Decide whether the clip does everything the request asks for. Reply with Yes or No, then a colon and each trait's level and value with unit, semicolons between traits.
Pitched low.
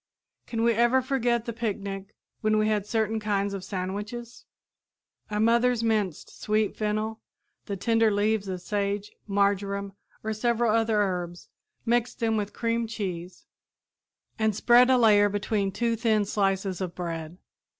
No: high, 215 Hz